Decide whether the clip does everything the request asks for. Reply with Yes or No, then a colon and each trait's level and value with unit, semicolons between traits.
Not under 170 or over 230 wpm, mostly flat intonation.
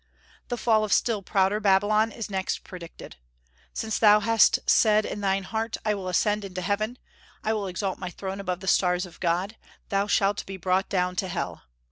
Yes: average, 190 wpm; narrow, 2.3 semitones